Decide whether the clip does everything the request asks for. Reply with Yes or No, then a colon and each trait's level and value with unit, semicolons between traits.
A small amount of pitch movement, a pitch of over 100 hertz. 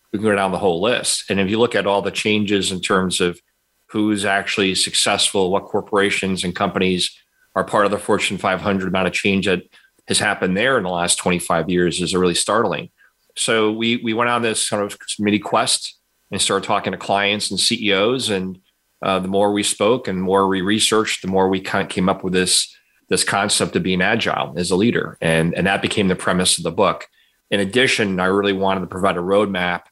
No: narrow, 1.8 semitones; very low, 95 Hz